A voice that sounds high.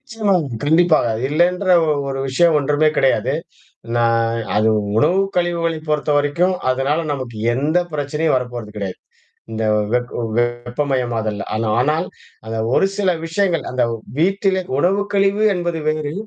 No: medium, 150 Hz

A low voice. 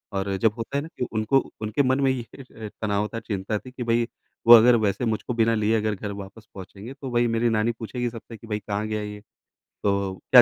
Yes: low, 110 Hz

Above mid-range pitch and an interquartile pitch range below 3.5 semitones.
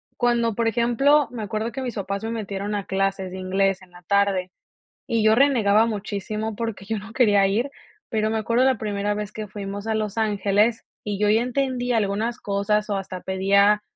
Yes: high, 210 Hz; narrow, 2.5 semitones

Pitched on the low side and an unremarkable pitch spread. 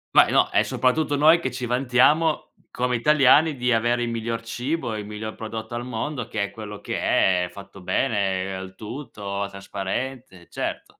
Yes: low, 115 Hz; average, 4.3 semitones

